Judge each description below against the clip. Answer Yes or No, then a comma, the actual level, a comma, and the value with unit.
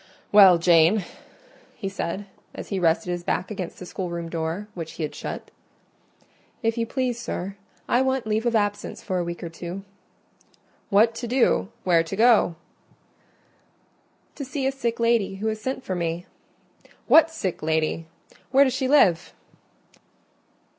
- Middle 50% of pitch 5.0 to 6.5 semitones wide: Yes, wide, 5.4 semitones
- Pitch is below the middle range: No, high, 195 Hz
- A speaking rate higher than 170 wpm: No, average, 150 wpm